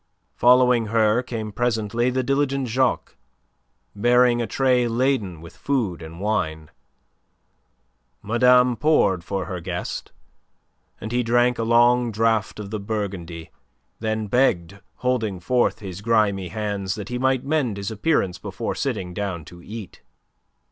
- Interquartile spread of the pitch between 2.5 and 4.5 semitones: Yes, average, 4.1 semitones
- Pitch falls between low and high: No, low, 110 Hz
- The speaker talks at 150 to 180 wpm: No, slow, 135 wpm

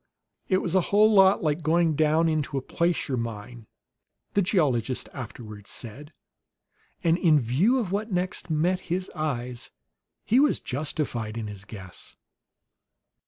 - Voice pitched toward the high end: No, medium, 155 Hz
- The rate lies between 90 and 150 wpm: Yes, average, 140 wpm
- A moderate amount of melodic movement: No, wide, 7.0 semitones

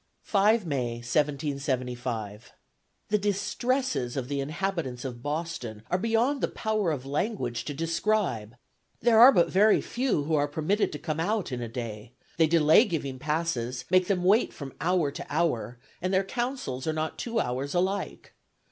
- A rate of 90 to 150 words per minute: No, average, 165 wpm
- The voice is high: No, medium, 155 Hz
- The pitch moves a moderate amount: No, wide, 7.5 semitones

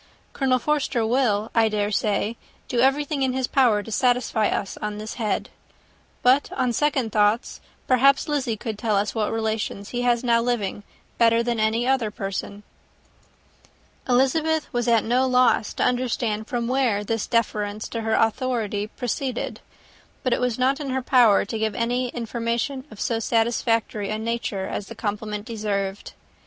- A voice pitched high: Yes, high, 230 Hz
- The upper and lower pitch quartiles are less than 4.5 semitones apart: Yes, average, 2.9 semitones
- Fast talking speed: No, average, 165 wpm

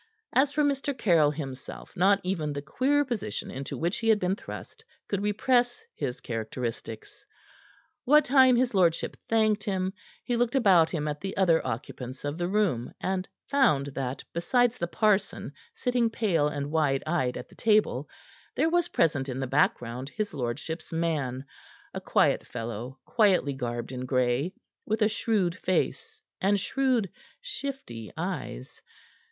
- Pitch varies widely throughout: Yes, wide, 8.8 semitones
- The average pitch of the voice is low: No, medium, 180 Hz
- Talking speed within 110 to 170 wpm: Yes, average, 155 wpm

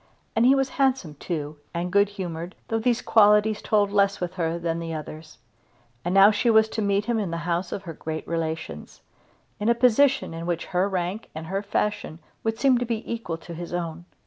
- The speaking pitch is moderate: No, high, 195 Hz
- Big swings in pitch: No, average, 4.6 semitones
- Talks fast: Yes, fast, 210 wpm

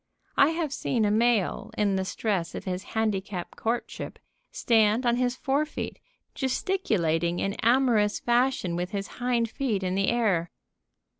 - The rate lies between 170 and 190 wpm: No, average, 150 wpm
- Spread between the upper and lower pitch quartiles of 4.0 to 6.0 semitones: Yes, average, 4.4 semitones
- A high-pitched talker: Yes, high, 220 Hz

